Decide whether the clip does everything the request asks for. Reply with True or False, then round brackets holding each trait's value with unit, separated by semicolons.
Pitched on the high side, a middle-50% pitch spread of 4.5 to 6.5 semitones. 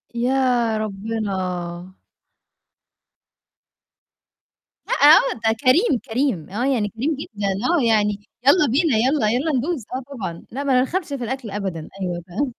True (235 Hz; 5.2 semitones)